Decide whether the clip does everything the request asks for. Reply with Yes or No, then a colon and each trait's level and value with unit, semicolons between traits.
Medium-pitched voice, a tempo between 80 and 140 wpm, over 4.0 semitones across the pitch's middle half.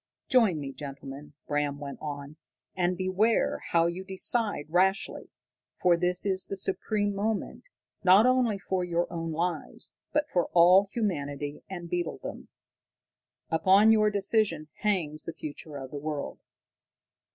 Yes: medium, 180 Hz; slow, 135 wpm; average, 4.7 semitones